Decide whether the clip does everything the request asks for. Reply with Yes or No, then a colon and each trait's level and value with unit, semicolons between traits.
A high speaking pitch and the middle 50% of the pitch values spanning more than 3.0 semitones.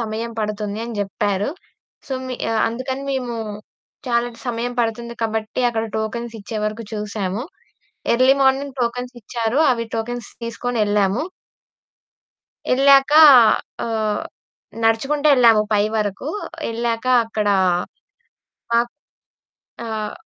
No: high, 230 Hz; narrow, 2.4 semitones